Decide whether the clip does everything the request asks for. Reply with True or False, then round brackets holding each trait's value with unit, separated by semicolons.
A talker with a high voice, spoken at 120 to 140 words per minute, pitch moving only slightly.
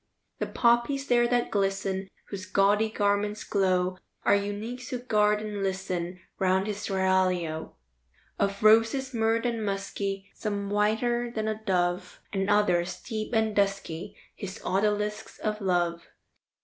True (205 Hz; 135 wpm; 2.3 semitones)